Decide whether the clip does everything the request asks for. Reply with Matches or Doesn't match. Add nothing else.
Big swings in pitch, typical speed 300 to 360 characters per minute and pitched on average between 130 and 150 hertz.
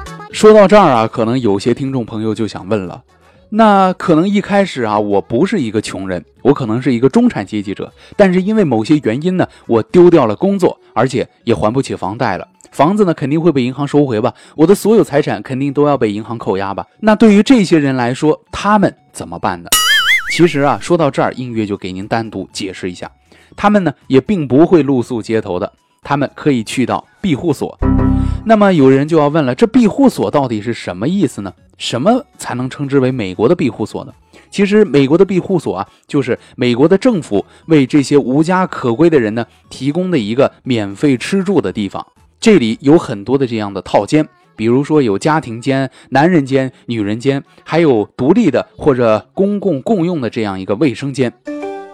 Matches